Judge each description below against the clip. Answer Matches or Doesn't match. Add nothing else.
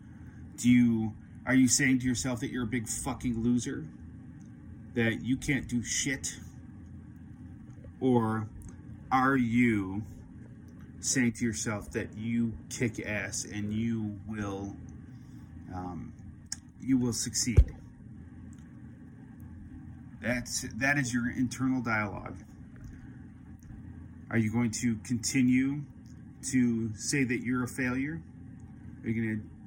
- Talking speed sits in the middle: Doesn't match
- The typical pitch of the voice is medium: Doesn't match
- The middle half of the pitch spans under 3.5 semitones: Matches